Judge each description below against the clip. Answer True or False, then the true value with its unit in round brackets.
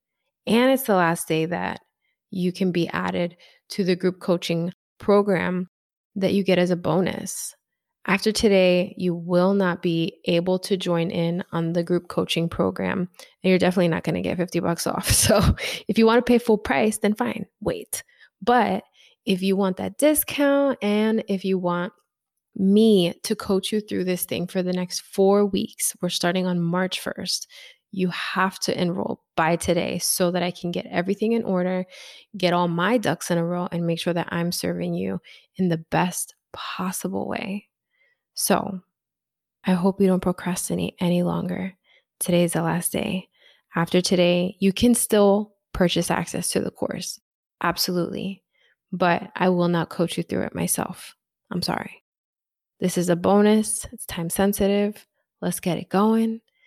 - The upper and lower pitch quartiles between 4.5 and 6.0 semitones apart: False (2.7 semitones)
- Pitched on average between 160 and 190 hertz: True (185 Hz)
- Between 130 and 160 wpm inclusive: False (170 wpm)